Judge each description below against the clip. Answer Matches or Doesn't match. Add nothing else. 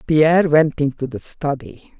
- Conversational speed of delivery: Matches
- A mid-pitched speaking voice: Matches